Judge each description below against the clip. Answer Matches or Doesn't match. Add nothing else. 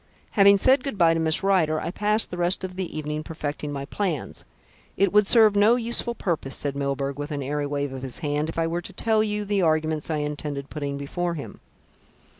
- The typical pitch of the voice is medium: Matches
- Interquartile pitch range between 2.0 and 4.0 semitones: Doesn't match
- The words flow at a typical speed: Doesn't match